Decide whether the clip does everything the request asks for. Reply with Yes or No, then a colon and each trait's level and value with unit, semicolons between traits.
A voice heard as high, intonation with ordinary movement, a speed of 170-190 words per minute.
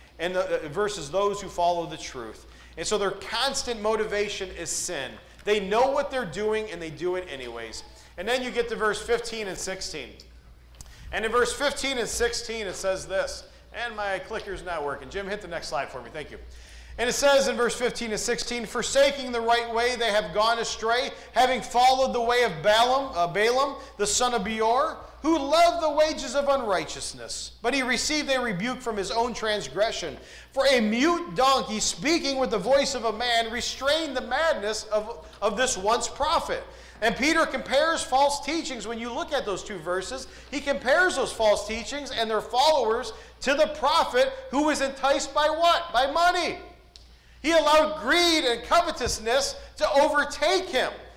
Yes: high, 240 Hz; average, 5.0 semitones; average, 185 wpm